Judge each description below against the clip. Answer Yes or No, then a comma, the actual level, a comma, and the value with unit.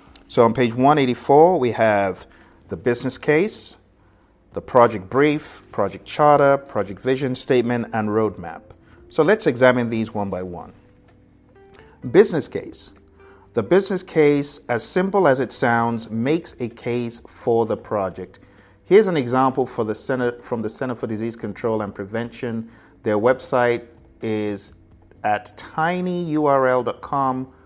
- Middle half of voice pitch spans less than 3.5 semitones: No, average, 4.1 semitones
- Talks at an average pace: No, slow, 125 wpm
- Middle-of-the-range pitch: No, low, 120 Hz